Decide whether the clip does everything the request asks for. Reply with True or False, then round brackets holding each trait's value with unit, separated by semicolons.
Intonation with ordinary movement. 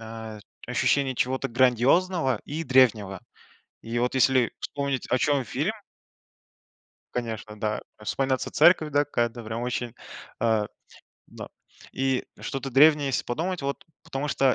True (3.2 semitones)